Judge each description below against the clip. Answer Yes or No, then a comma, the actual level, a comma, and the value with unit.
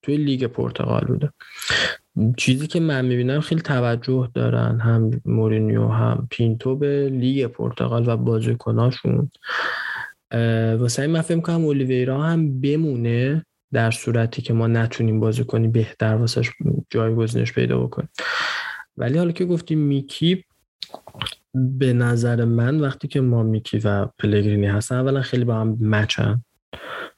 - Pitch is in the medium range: No, low, 120 Hz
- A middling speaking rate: Yes, average, 130 wpm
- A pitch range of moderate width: Yes, average, 3.6 semitones